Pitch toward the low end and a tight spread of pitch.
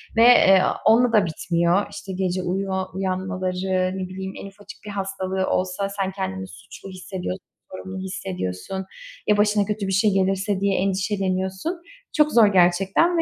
No: high, 190 Hz; narrow, 1.4 semitones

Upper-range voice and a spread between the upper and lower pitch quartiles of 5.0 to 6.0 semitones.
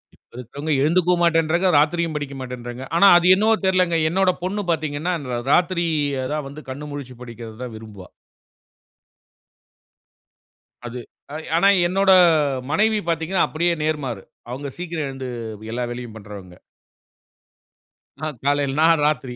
No: medium, 150 Hz; average, 5.3 semitones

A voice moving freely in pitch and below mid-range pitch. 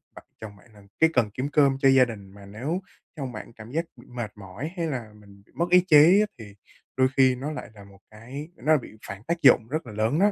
Yes: wide, 6.0 semitones; low, 125 Hz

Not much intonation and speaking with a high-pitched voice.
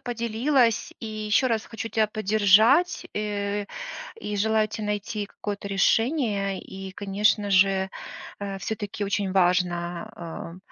Yes: narrow, 2.1 semitones; high, 205 Hz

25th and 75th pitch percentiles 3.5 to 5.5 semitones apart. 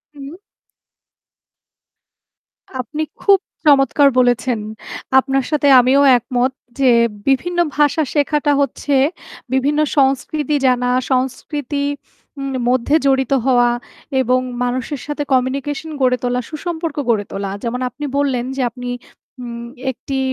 No: average, 2.8 semitones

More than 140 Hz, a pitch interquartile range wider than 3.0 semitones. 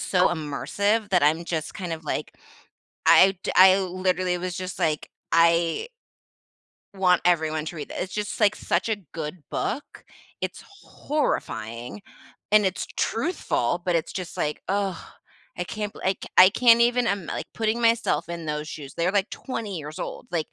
Yes: medium, 185 Hz; average, 4.1 semitones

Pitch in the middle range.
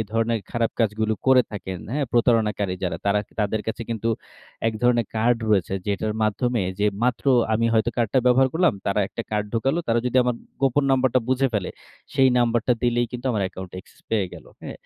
No: low, 115 Hz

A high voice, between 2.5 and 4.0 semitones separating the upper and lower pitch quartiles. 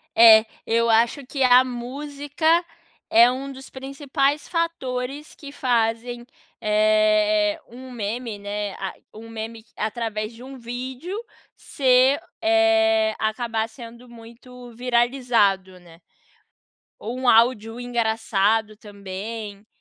Yes: high, 235 Hz; average, 3.3 semitones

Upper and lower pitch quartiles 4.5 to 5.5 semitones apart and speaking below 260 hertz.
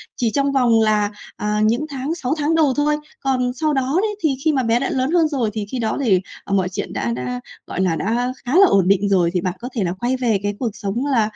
Yes: average, 5.2 semitones; high, 240 Hz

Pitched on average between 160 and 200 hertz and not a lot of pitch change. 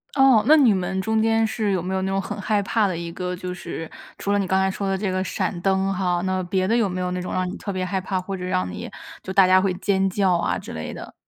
Yes: high, 190 Hz; narrow, 1.7 semitones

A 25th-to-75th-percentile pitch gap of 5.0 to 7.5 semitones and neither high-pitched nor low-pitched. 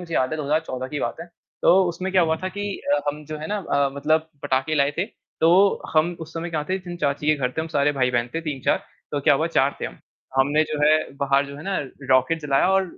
No: average, 2.9 semitones; medium, 155 Hz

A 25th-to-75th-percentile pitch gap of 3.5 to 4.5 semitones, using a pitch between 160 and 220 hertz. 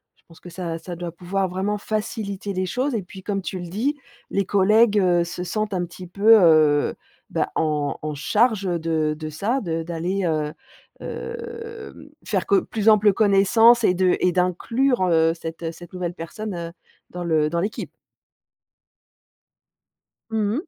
Yes: average, 4.2 semitones; medium, 185 Hz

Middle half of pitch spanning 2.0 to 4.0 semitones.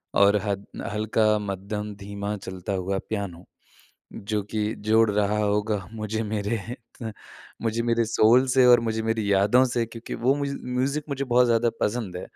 Yes: narrow, 2.5 semitones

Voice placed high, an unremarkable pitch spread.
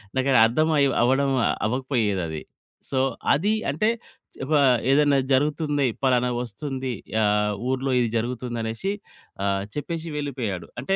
No: low, 130 Hz; average, 3.6 semitones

